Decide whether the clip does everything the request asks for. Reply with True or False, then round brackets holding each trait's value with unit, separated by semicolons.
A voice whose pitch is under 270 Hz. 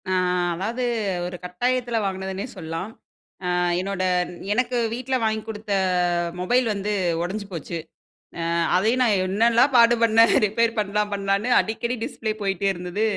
True (210 Hz)